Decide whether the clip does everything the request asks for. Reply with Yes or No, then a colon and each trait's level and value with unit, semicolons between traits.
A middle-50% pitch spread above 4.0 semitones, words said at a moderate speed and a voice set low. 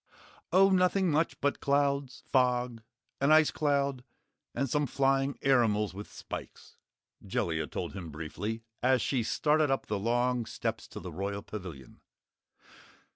No: wide, 5.4 semitones; slow, 130 wpm; low, 125 Hz